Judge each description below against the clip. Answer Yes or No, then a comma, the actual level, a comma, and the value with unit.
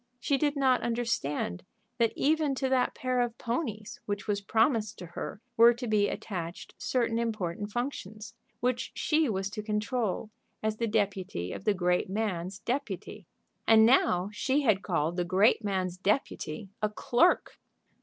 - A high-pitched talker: Yes, high, 215 Hz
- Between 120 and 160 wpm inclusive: Yes, average, 155 wpm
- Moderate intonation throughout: Yes, average, 4.0 semitones